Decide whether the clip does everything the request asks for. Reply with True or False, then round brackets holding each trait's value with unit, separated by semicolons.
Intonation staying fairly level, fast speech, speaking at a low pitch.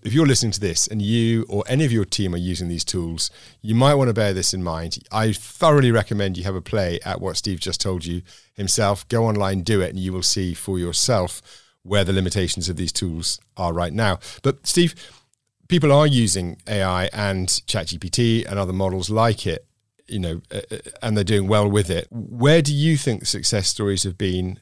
False (3.7 semitones; 210 wpm; 100 Hz)